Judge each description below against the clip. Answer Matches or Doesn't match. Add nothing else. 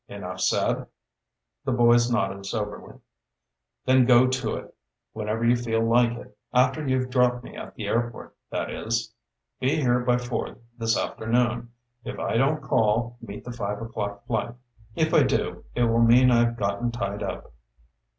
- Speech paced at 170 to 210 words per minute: Doesn't match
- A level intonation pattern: Matches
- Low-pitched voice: Matches